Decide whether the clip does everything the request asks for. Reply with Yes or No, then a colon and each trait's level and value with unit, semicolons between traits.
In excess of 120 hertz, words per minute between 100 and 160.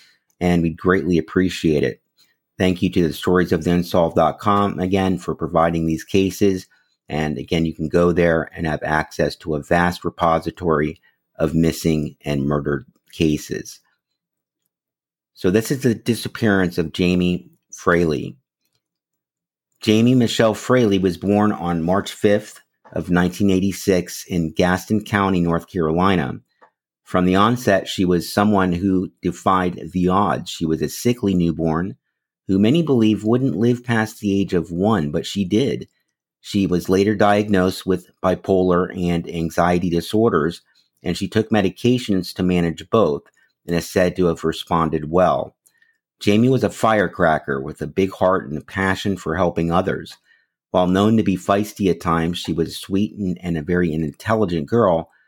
No: very low, 90 Hz; average, 150 wpm